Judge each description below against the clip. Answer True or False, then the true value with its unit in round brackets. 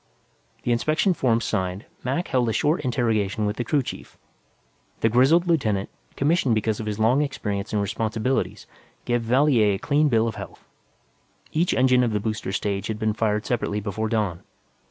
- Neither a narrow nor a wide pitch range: True (3.7 semitones)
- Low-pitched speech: True (115 Hz)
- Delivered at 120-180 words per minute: True (175 wpm)